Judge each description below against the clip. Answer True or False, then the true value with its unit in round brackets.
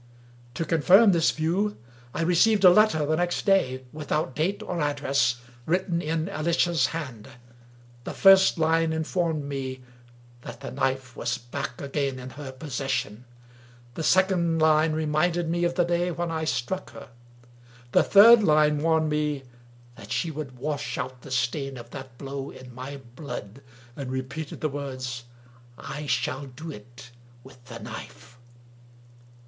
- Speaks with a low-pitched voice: False (150 Hz)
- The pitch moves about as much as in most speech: True (4.2 semitones)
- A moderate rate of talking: True (155 wpm)